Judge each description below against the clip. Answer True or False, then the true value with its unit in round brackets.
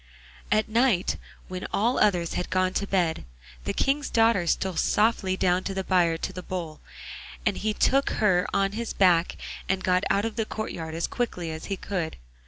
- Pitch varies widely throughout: False (3.4 semitones)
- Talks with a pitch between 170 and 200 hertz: True (190 Hz)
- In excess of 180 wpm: True (190 wpm)